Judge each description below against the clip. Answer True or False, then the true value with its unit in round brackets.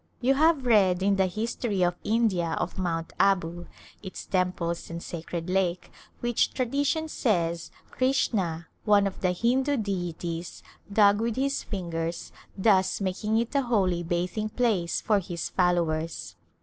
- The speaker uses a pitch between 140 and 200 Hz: True (190 Hz)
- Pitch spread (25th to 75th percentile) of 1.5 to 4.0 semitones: False (4.8 semitones)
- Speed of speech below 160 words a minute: True (140 wpm)